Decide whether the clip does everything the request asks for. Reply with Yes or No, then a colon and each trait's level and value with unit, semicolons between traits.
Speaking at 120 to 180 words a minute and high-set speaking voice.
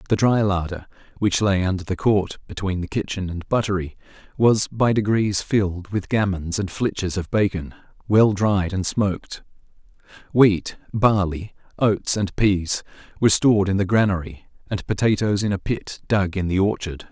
No: average, 160 wpm; low, 100 Hz